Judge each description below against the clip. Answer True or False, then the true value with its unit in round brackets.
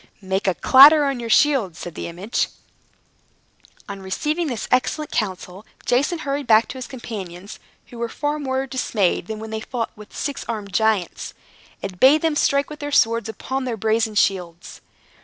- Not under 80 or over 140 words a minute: False (175 wpm)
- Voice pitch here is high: True (230 Hz)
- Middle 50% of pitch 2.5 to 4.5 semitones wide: False (5.6 semitones)